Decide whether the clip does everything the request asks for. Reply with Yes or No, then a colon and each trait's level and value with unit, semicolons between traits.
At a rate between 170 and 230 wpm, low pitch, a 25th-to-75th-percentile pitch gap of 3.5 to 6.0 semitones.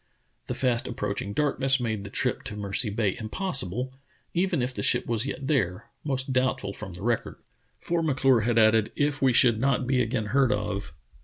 Yes: average, 200 wpm; low, 120 Hz; average, 4.2 semitones